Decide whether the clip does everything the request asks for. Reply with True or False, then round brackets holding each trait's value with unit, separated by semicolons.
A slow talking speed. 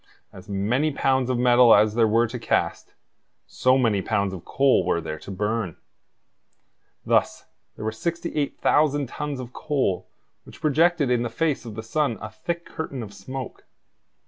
False (165 wpm)